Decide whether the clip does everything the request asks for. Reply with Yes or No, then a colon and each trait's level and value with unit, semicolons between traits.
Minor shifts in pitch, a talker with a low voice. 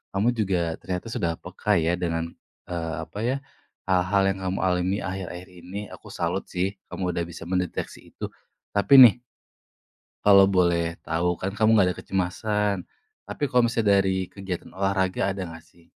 Yes: narrow, 2.2 semitones; very low, 95 Hz